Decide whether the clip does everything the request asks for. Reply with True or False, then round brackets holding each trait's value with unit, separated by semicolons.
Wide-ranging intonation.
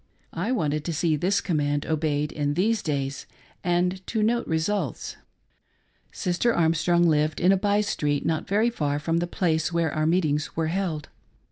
False (3.7 semitones)